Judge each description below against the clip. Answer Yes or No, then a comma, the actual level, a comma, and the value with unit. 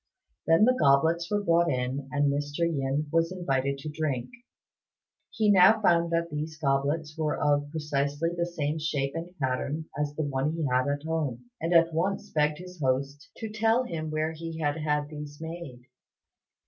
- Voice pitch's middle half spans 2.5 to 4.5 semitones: Yes, average, 2.8 semitones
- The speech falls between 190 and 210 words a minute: No, average, 175 wpm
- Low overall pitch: No, medium, 155 Hz